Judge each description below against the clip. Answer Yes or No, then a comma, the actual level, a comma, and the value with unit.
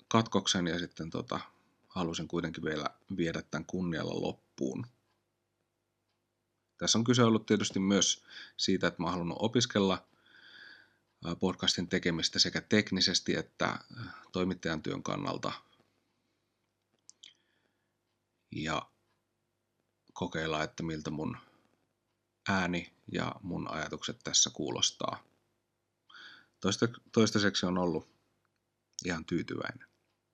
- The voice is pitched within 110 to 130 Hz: No, very low, 95 Hz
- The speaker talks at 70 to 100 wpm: Yes, slow, 95 wpm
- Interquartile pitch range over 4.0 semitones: Yes, average, 4.4 semitones